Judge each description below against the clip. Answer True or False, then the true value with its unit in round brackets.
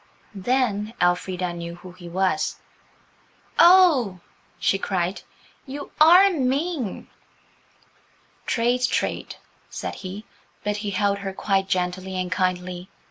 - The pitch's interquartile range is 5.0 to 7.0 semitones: True (5.4 semitones)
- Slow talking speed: True (110 wpm)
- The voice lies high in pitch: True (195 Hz)